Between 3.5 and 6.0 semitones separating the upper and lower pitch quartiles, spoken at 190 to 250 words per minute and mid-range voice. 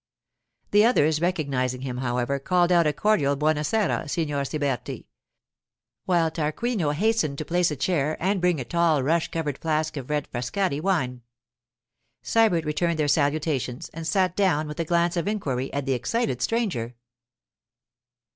No: average, 4.1 semitones; average, 155 wpm; medium, 155 Hz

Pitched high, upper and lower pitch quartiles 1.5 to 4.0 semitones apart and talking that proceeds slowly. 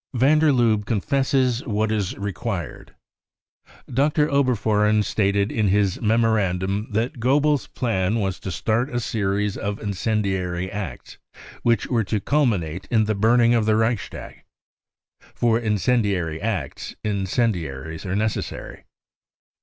No: low, 110 Hz; average, 3.3 semitones; slow, 125 wpm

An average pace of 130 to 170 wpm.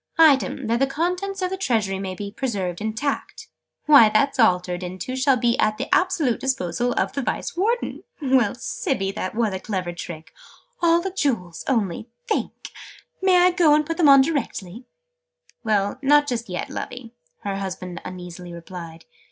Yes: average, 165 wpm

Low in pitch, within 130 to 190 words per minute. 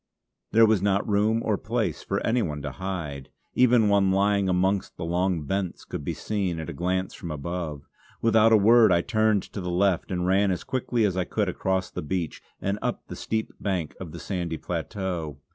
No: very low, 95 Hz; fast, 205 wpm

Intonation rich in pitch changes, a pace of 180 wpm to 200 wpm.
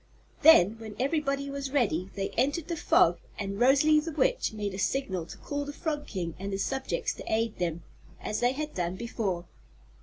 Yes: wide, 6.7 semitones; average, 190 wpm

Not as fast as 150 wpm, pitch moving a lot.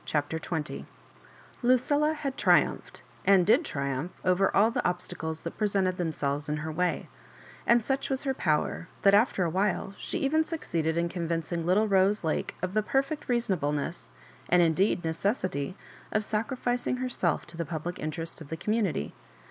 No: average, 165 wpm; wide, 5.8 semitones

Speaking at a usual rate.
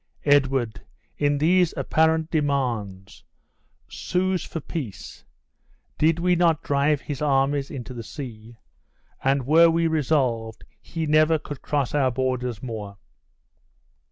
No: slow, 120 wpm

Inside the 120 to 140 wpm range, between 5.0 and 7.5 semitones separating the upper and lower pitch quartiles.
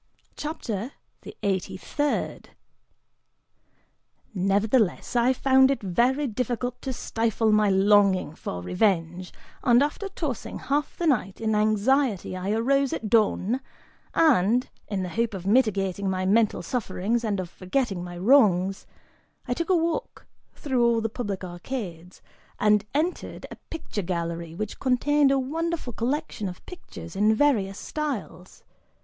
Yes: slow, 135 wpm; wide, 5.6 semitones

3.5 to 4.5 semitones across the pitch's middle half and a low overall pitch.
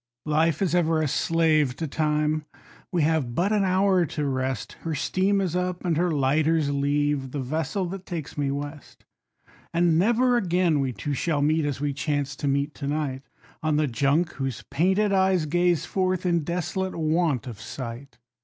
No: average, 3.8 semitones; medium, 155 Hz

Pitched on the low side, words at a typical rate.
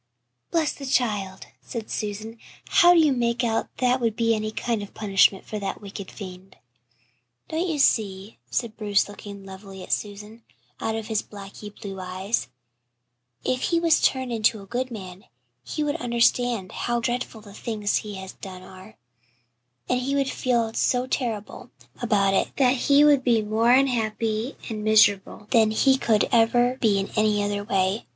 No: high, 220 Hz; average, 175 wpm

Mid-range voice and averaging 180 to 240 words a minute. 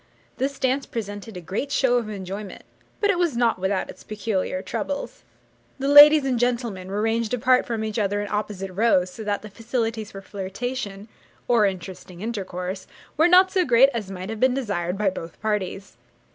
No: high, 215 Hz; average, 185 wpm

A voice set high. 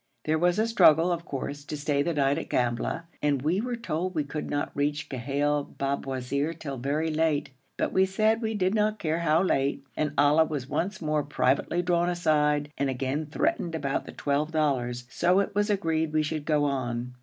No: medium, 155 Hz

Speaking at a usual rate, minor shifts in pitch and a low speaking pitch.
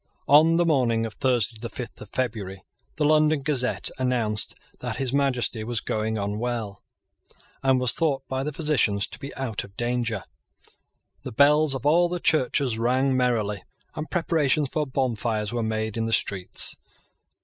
No: average, 165 wpm; average, 4.3 semitones; low, 125 Hz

